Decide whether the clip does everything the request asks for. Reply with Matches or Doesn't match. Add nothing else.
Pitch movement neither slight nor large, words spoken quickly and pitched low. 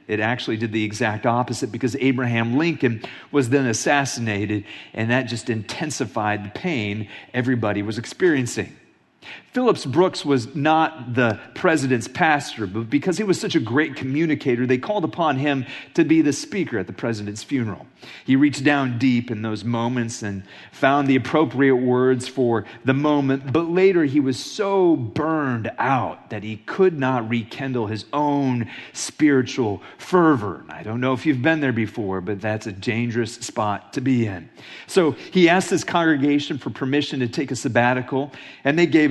Doesn't match